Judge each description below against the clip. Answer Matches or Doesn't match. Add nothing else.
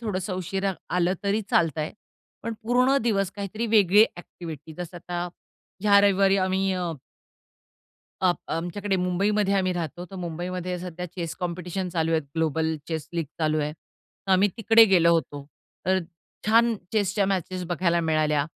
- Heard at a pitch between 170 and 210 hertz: Matches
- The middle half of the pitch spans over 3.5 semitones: Doesn't match